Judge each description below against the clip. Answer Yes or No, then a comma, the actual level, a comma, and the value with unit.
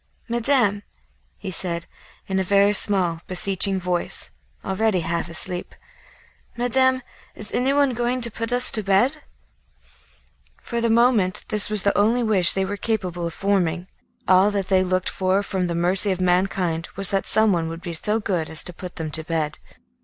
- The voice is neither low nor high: No, high, 195 Hz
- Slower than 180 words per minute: Yes, average, 170 wpm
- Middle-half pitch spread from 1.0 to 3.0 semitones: No, average, 3.6 semitones